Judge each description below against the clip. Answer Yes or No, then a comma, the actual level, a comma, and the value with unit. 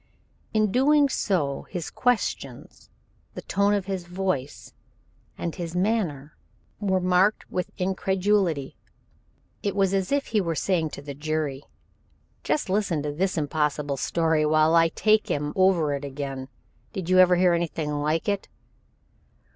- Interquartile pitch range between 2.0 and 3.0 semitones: No, average, 4.5 semitones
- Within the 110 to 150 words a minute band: Yes, average, 145 wpm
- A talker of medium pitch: Yes, medium, 175 Hz